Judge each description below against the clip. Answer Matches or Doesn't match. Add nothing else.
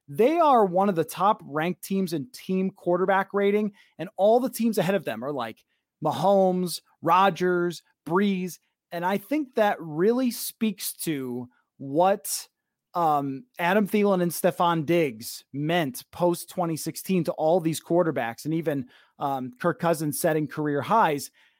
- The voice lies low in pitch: Doesn't match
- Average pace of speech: Matches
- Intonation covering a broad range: Doesn't match